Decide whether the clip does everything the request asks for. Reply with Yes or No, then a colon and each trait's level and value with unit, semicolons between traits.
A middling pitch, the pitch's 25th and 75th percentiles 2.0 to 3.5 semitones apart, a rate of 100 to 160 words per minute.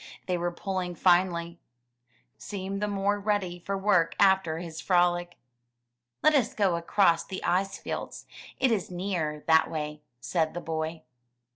Yes: medium, 180 Hz; average, 2.7 semitones; average, 150 wpm